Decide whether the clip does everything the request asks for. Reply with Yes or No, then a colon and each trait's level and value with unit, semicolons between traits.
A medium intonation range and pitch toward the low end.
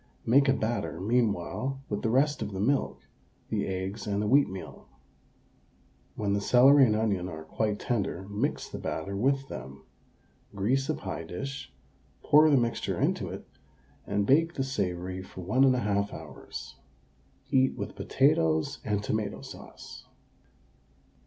No: wide, 5.7 semitones; low, 105 Hz